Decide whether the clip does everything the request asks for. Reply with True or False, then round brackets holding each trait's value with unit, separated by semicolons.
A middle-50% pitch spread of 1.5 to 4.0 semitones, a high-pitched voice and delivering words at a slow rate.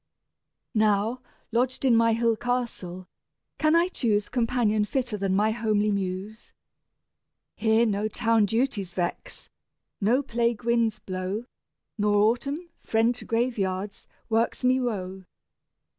True (2.7 semitones; 225 Hz; 120 wpm)